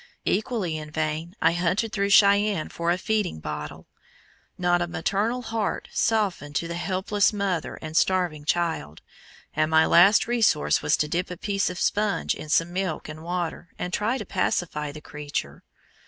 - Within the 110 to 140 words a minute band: No, average, 170 wpm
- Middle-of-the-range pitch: Yes, medium, 175 Hz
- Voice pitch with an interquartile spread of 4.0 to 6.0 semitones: Yes, average, 4.3 semitones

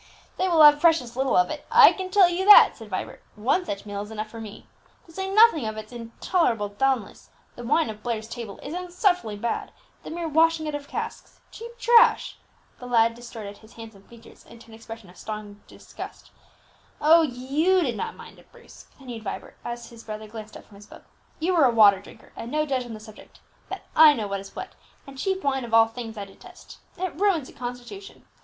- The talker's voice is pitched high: Yes, high, 240 Hz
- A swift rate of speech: Yes, fast, 215 wpm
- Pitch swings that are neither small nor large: No, wide, 7.0 semitones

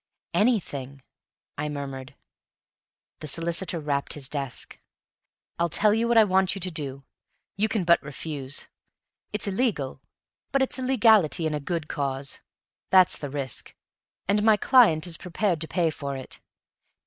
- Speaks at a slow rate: No, average, 150 wpm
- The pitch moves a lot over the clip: Yes, wide, 6.5 semitones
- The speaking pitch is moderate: Yes, medium, 165 Hz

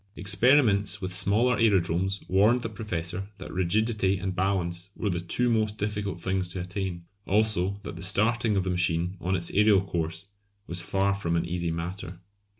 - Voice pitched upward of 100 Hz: No, very low, 95 Hz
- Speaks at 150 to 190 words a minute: Yes, average, 170 wpm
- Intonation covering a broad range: No, average, 2.9 semitones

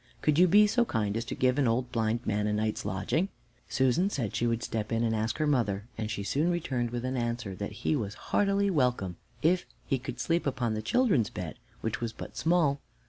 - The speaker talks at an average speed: No, fast, 225 wpm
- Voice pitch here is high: No, low, 120 Hz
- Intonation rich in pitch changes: Yes, wide, 5.8 semitones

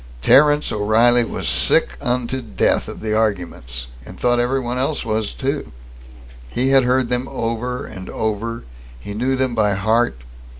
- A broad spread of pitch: No, average, 3.1 semitones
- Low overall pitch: Yes, low, 120 Hz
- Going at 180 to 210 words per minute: No, average, 155 wpm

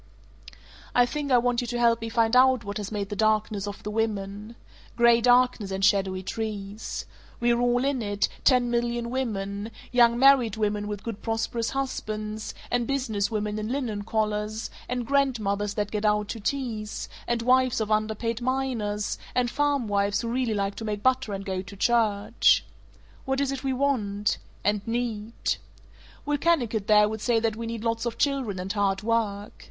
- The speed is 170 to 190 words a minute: Yes, average, 180 wpm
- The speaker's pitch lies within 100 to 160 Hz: No, high, 225 Hz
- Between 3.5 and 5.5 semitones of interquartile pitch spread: No, average, 2.8 semitones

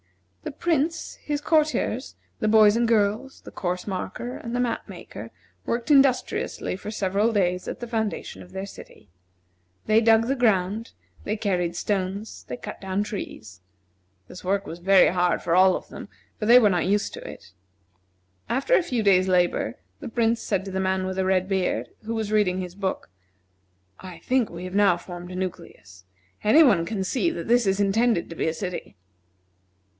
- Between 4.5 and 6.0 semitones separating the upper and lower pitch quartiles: No, average, 3.9 semitones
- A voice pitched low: No, high, 200 Hz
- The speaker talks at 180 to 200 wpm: Yes, average, 185 wpm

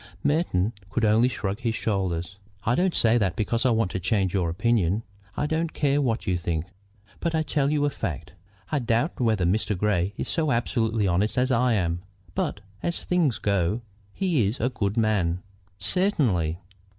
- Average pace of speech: Yes, average, 180 wpm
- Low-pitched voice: Yes, low, 110 Hz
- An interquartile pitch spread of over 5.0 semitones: Yes, wide, 5.6 semitones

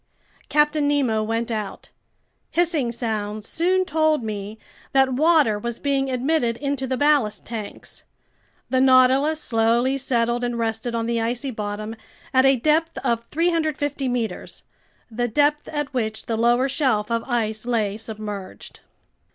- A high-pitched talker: Yes, high, 245 Hz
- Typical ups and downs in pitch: Yes, average, 4.3 semitones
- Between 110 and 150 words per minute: Yes, average, 140 wpm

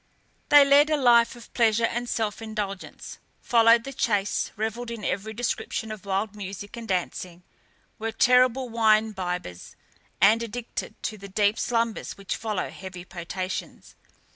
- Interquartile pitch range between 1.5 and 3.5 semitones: Yes, average, 2.9 semitones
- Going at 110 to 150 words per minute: Yes, average, 145 wpm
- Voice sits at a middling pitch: No, high, 220 Hz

